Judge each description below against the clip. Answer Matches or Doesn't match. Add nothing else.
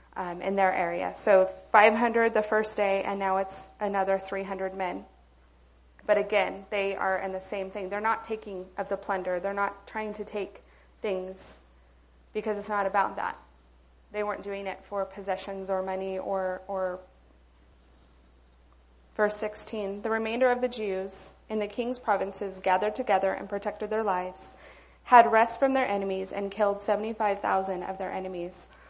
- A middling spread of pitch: Doesn't match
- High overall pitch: Matches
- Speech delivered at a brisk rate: Doesn't match